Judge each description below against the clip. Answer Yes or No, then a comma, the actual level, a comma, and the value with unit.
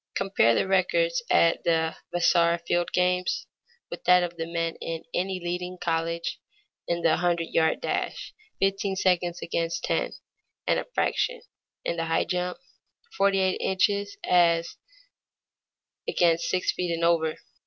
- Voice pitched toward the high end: No, medium, 175 Hz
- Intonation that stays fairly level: Yes, narrow, 1.8 semitones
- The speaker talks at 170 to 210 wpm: No, average, 145 wpm